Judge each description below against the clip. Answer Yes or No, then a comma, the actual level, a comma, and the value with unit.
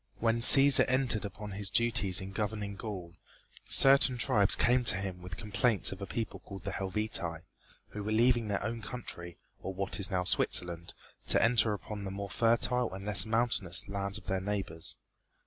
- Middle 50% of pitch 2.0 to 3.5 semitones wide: Yes, average, 3.2 semitones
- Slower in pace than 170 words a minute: No, average, 180 wpm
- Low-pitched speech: Yes, low, 100 Hz